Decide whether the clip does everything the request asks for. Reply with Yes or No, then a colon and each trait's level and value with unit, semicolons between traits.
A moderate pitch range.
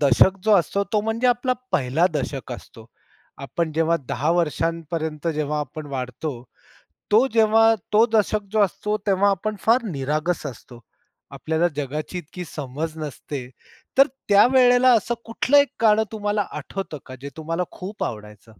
No: wide, 6.4 semitones